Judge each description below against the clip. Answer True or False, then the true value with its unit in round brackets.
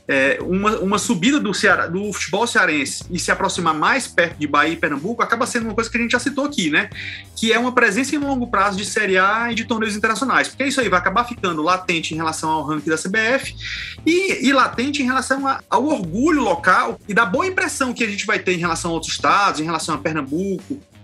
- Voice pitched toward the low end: False (215 Hz)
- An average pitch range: False (6.8 semitones)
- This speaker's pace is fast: True (235 wpm)